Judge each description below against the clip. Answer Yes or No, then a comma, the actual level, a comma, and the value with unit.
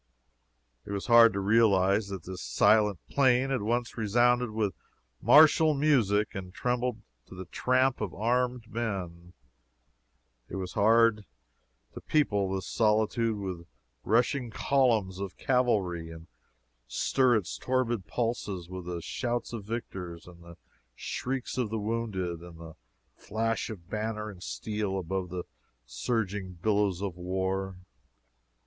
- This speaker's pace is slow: Yes, slow, 130 wpm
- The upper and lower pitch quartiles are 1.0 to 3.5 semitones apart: No, average, 4.2 semitones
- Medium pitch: No, low, 105 Hz